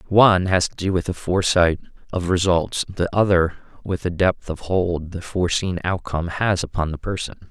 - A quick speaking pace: No, average, 185 wpm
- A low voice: Yes, very low, 90 Hz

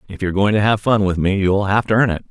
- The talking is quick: Yes, fast, 340 wpm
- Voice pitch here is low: Yes, low, 100 Hz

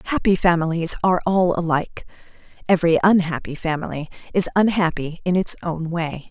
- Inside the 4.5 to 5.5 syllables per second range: No, 5.7 syllables/s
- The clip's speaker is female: Yes, female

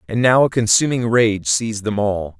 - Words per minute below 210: Yes, average, 200 wpm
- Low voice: Yes, low, 110 Hz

